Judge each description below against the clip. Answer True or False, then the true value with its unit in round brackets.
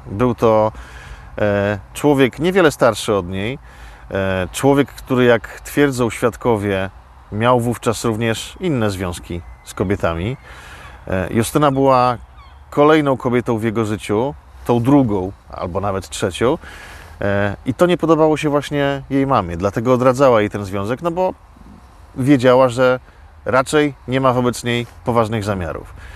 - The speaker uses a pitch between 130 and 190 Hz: False (115 Hz)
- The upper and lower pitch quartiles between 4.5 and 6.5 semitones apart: True (5.4 semitones)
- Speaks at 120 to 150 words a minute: True (135 wpm)